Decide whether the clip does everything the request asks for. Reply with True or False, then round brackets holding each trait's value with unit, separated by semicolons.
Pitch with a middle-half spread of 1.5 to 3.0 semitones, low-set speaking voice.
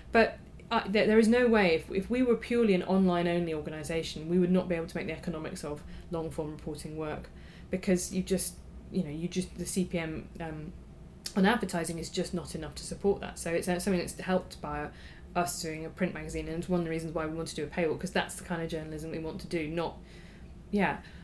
False (2.6 semitones; 175 Hz)